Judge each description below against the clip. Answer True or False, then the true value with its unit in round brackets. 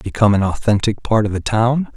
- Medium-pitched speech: False (110 Hz)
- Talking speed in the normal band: False (215 wpm)